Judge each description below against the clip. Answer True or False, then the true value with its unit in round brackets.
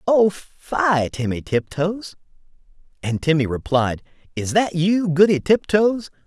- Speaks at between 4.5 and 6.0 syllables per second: False (4.1 syllables/s)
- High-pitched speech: False (170 Hz)